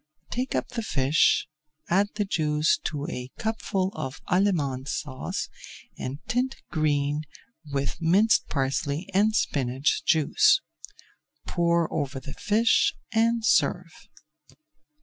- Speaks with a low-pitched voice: No, medium, 165 Hz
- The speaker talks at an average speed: No, slow, 110 wpm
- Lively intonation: Yes, wide, 6.5 semitones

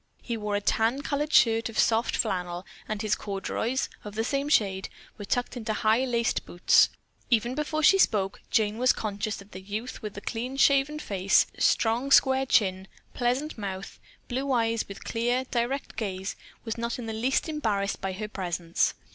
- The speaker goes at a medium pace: Yes, average, 180 wpm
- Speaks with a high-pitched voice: Yes, high, 225 Hz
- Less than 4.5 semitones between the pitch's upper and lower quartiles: Yes, average, 3.9 semitones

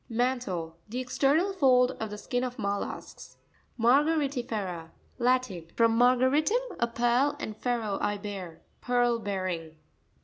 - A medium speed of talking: No, slow, 125 wpm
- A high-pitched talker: Yes, high, 240 Hz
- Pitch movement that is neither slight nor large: Yes, average, 4.0 semitones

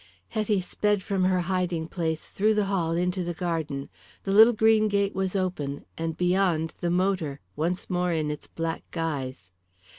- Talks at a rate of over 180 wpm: No, average, 170 wpm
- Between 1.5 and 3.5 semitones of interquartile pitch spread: Yes, average, 3.2 semitones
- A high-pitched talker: No, medium, 180 Hz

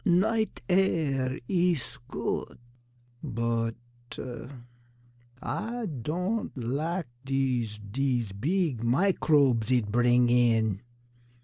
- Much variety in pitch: Yes, wide, 6.9 semitones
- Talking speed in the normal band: No, slow, 80 wpm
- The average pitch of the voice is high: No, low, 130 Hz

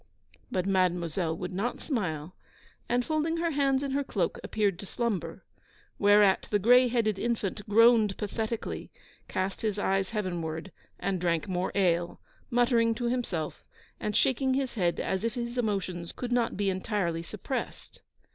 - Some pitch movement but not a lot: Yes, average, 4.6 semitones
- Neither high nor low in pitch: No, high, 210 Hz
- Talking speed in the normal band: Yes, average, 150 wpm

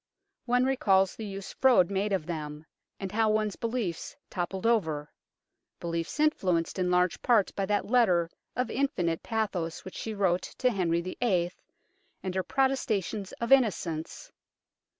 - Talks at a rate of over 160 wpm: No, average, 145 wpm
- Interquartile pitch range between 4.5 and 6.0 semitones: Yes, average, 4.8 semitones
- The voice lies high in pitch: Yes, high, 195 Hz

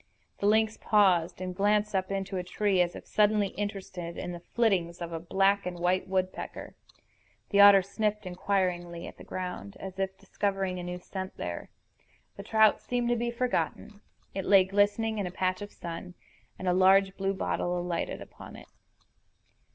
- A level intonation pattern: Yes, narrow, 2.2 semitones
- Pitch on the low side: No, high, 190 Hz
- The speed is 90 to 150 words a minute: No, average, 175 wpm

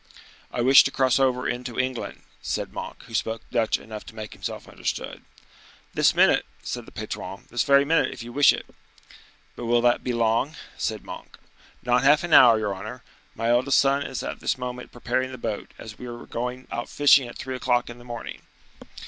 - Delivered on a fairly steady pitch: Yes, narrow, 1.9 semitones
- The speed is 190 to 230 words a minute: Yes, average, 200 wpm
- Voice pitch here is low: Yes, low, 125 Hz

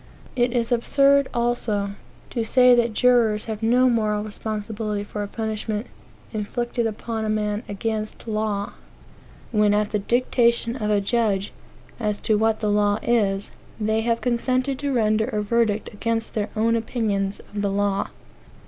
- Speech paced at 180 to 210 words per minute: No, average, 155 wpm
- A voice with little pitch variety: Yes, narrow, 2.1 semitones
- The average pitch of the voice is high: Yes, high, 220 Hz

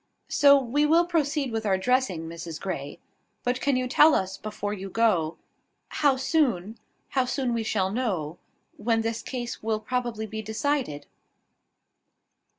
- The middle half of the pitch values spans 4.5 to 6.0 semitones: Yes, average, 5.2 semitones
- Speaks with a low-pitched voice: No, high, 230 Hz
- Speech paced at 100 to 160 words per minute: Yes, average, 150 wpm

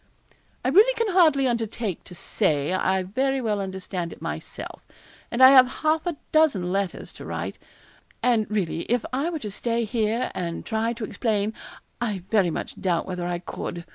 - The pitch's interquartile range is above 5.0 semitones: Yes, wide, 5.6 semitones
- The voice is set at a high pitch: Yes, high, 220 Hz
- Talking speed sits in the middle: Yes, average, 175 wpm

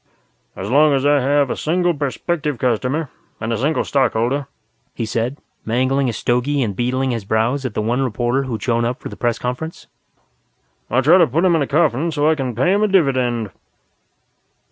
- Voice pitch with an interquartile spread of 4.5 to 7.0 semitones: No, average, 3.6 semitones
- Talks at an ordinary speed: Yes, average, 195 wpm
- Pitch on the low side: Yes, low, 130 Hz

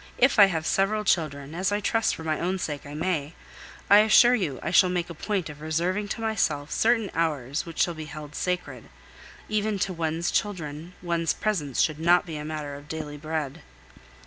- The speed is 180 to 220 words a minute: Yes, average, 200 wpm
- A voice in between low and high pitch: Yes, medium, 165 Hz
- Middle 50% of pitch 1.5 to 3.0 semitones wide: No, average, 4.2 semitones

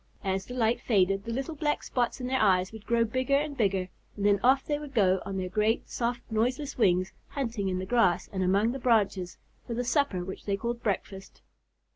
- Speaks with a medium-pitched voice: No, high, 220 Hz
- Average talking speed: No, fast, 215 wpm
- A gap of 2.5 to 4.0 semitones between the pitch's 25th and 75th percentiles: No, average, 4.5 semitones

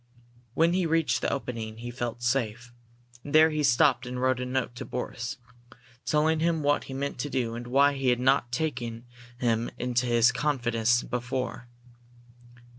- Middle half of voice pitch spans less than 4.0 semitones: Yes, average, 3.0 semitones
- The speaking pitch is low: Yes, low, 125 Hz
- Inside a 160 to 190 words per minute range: Yes, average, 170 wpm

